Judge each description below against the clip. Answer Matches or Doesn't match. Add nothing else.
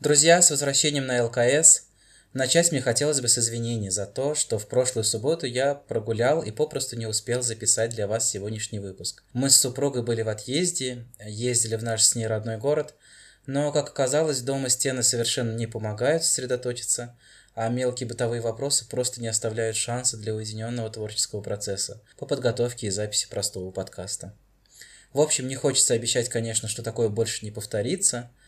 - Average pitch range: Matches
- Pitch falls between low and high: Doesn't match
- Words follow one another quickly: Matches